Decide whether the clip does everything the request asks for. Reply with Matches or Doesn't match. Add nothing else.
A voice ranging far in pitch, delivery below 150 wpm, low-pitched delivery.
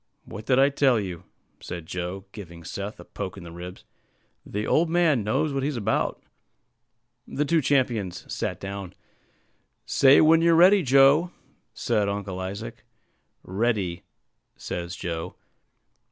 Matches